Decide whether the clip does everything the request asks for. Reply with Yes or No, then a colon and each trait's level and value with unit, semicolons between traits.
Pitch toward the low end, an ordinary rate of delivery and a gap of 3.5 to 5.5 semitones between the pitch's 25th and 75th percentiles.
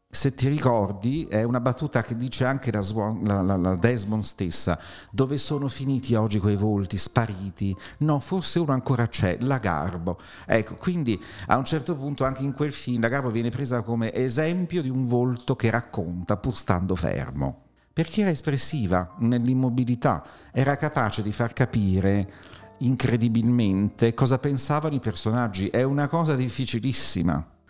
Yes: low, 120 Hz; average, 155 wpm; average, 4.8 semitones